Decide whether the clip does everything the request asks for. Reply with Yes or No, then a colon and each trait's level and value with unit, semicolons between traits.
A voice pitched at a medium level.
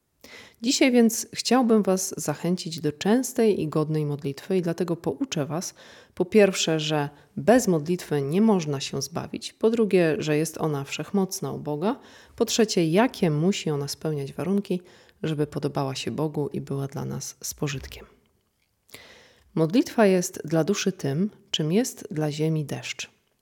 Yes: medium, 170 Hz